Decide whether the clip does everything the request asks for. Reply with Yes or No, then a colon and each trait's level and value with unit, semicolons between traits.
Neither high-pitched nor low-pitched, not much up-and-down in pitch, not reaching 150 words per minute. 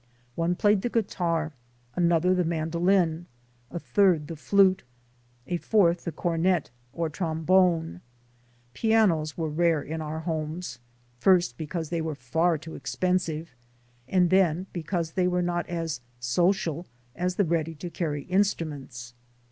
Yes: medium, 170 Hz; narrow, 2.3 semitones; average, 140 wpm